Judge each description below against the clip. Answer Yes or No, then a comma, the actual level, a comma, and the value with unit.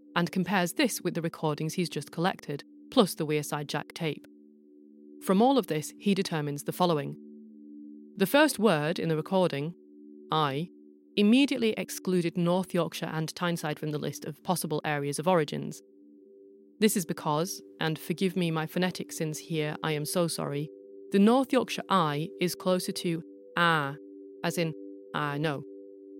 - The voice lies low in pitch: No, medium, 160 Hz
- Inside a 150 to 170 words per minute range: Yes, average, 160 wpm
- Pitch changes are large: Yes, wide, 5.7 semitones